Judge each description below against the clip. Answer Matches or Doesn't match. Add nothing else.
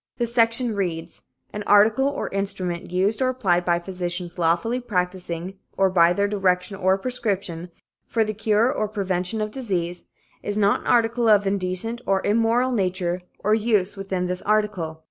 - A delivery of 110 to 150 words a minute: Doesn't match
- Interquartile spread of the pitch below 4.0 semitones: Matches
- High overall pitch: Matches